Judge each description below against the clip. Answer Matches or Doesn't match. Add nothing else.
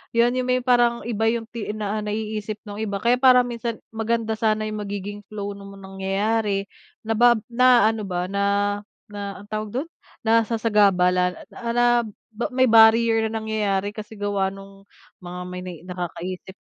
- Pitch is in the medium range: Doesn't match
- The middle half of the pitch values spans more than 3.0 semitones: Doesn't match